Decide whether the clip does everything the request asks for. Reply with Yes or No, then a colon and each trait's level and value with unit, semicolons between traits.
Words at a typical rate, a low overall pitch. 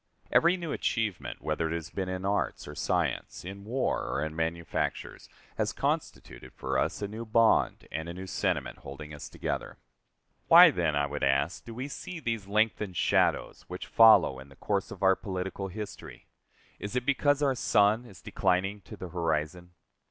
Yes: average, 180 wpm; very low, 95 Hz